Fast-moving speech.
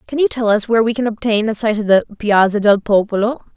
Yes: fast, 255 wpm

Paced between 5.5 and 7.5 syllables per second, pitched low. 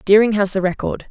No: 5.9 syllables/s; high, 200 Hz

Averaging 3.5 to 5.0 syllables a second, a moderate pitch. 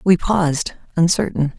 Yes: 4.7 syllables/s; medium, 170 Hz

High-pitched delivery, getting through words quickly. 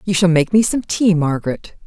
No: medium, 180 Hz; fast, 225 wpm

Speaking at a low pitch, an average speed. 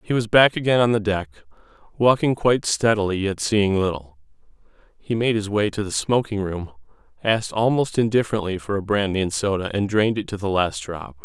Yes: low, 105 Hz; average, 190 wpm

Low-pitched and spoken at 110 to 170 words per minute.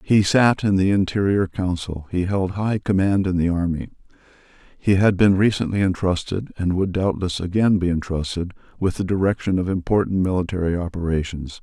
Yes: very low, 95 Hz; average, 160 wpm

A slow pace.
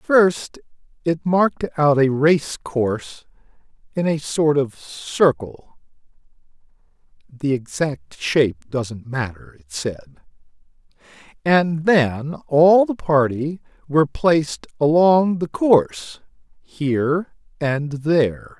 Yes: slow, 105 wpm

